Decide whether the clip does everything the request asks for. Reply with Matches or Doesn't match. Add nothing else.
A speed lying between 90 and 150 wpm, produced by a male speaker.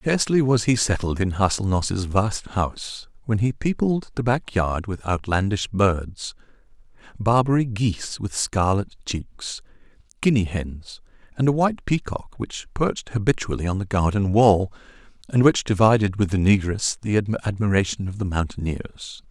Matches